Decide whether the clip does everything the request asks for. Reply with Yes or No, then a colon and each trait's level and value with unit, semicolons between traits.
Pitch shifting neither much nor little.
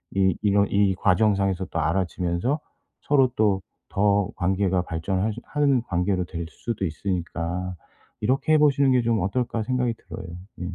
Yes: average, 4.4 semitones